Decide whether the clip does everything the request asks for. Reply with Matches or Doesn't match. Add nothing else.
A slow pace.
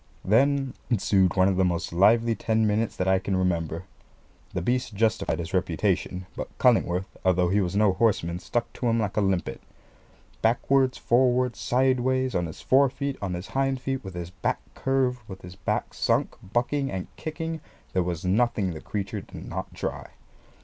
Doesn't match